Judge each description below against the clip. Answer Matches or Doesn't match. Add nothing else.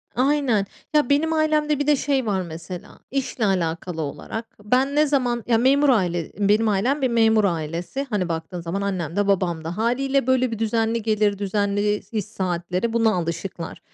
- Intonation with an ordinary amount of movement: Doesn't match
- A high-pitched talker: Matches